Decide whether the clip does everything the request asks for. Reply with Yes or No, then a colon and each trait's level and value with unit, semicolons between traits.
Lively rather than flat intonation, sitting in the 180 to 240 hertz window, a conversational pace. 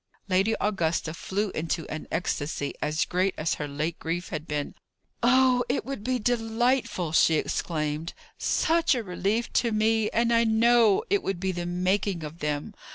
Yes: wide, 6.1 semitones; high, 190 Hz; average, 165 wpm